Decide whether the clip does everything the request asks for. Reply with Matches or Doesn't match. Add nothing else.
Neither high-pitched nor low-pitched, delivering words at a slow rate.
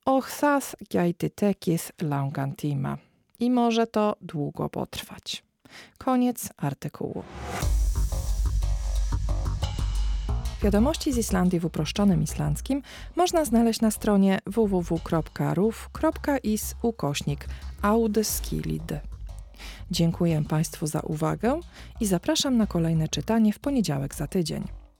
Matches